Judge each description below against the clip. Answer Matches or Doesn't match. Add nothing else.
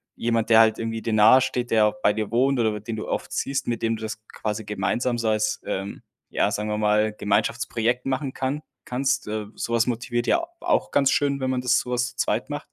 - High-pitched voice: Doesn't match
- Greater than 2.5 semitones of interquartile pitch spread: Matches